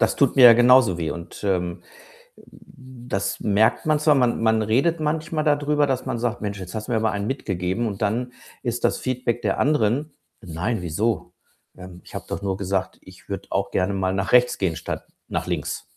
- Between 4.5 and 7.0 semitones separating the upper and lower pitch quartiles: Yes, average, 5.0 semitones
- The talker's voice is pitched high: No, low, 110 Hz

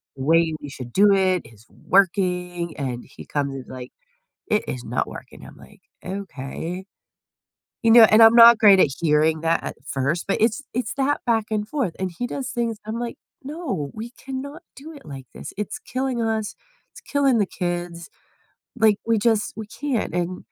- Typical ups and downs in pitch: No, wide, 6.0 semitones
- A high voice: Yes, high, 200 Hz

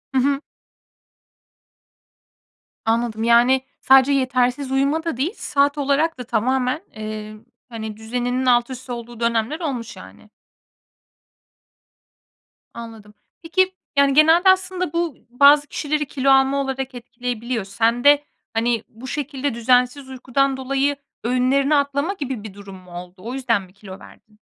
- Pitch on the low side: No, very high, 255 Hz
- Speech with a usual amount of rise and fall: Yes, average, 3.4 semitones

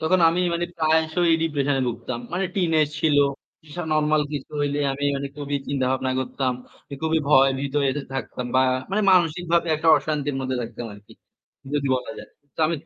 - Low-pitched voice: No, medium, 150 Hz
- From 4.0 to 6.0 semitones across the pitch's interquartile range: No, average, 3.3 semitones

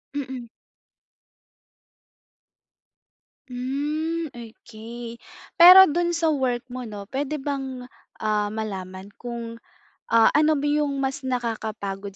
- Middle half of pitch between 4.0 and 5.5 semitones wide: Yes, average, 4.7 semitones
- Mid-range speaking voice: No, very high, 250 Hz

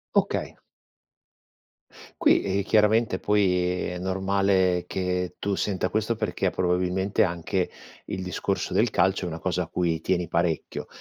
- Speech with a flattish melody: Yes, narrow, 1.6 semitones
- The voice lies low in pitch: Yes, very low, 95 Hz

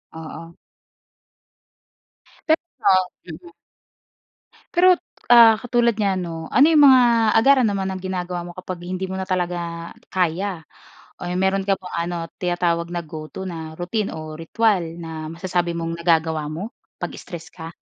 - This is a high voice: No, medium, 175 Hz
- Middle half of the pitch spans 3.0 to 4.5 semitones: No, narrow, 2.5 semitones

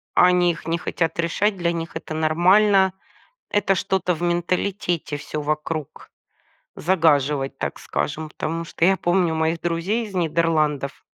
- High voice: No, medium, 170 Hz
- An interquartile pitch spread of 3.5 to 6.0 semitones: No, narrow, 2.6 semitones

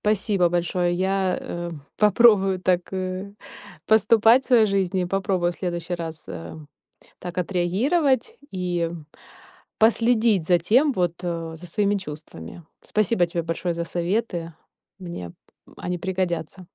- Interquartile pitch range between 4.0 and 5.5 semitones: No, average, 3.2 semitones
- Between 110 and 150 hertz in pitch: No, medium, 185 Hz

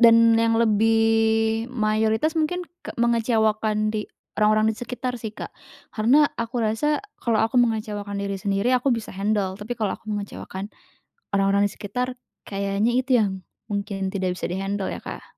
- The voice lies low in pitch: No, high, 220 Hz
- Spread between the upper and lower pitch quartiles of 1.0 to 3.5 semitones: Yes, narrow, 2.5 semitones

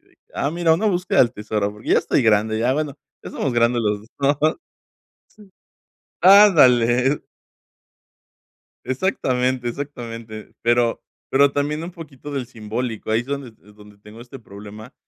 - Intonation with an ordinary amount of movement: Yes, average, 4.5 semitones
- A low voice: Yes, low, 125 Hz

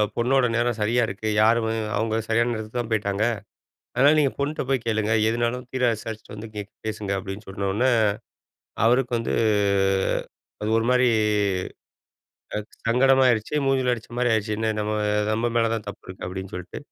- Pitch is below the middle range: Yes, low, 115 Hz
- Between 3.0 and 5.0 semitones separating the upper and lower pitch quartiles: No, narrow, 2.6 semitones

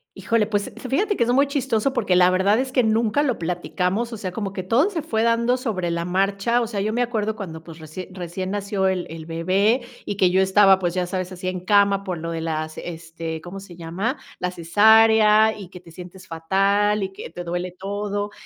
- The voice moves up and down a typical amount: Yes, average, 3.7 semitones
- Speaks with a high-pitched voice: Yes, high, 195 Hz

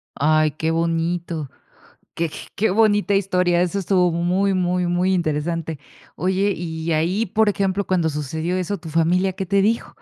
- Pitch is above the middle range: No, medium, 175 Hz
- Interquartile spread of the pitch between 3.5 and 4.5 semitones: No, average, 2.8 semitones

